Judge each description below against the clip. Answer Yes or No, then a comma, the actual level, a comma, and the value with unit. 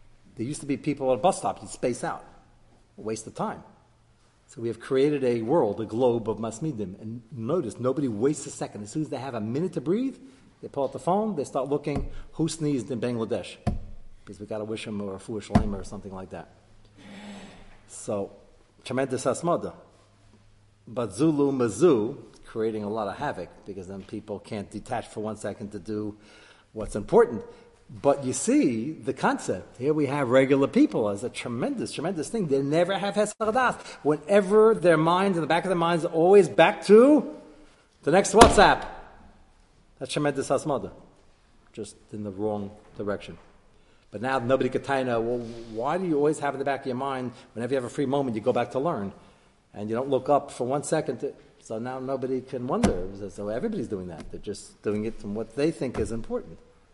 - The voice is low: Yes, low, 130 Hz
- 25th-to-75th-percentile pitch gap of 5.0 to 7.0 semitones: Yes, wide, 5.5 semitones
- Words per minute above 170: Yes, average, 200 wpm